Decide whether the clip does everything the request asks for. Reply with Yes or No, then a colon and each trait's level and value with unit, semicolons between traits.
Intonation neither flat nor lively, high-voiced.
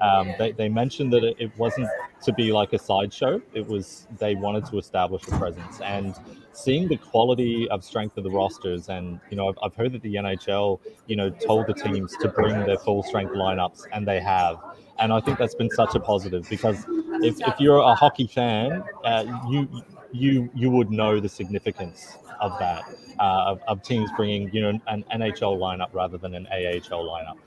No: average, 3.5 semitones; low, 110 Hz